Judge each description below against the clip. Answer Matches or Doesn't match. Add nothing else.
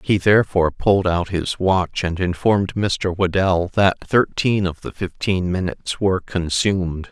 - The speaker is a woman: Doesn't match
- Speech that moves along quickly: Doesn't match